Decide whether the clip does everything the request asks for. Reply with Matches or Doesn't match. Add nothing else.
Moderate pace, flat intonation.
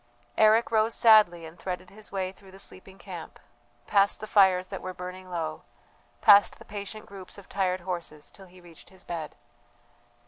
Matches